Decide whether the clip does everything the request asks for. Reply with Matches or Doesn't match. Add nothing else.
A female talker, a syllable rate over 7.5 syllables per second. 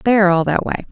Matches